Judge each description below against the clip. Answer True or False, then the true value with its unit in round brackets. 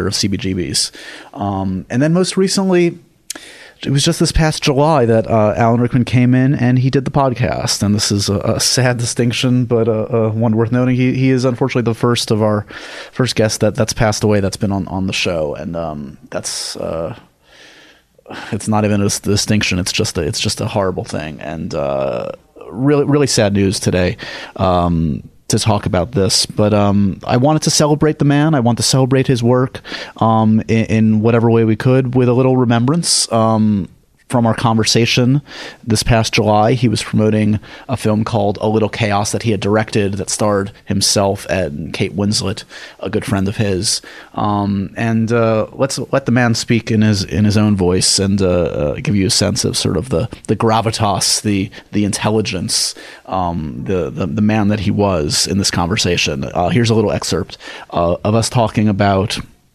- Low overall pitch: True (110 Hz)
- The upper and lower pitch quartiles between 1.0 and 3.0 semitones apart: False (3.5 semitones)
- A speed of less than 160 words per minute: False (195 wpm)